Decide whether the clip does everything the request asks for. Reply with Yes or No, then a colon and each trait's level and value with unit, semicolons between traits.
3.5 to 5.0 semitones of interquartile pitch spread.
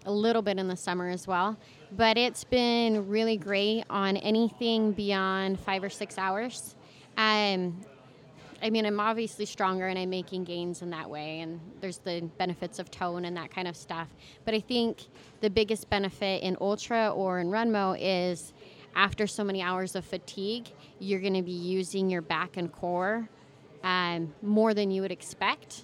No: average, 3.0 semitones